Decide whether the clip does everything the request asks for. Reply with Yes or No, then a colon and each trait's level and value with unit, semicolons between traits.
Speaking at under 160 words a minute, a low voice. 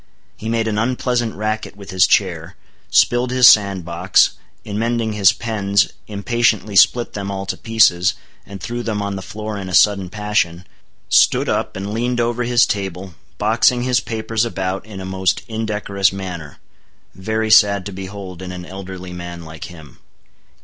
No: average, 170 wpm; low, 100 Hz